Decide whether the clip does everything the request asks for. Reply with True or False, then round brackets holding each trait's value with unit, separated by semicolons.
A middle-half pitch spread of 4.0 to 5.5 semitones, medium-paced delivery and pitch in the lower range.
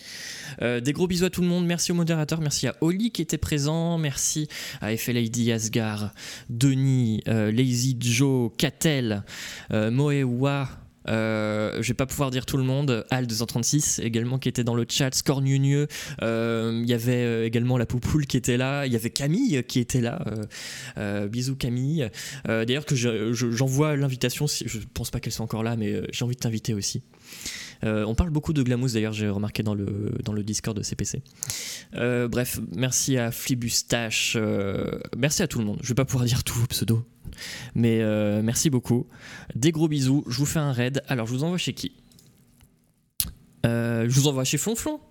False (3.6 semitones; 195 wpm; 125 Hz)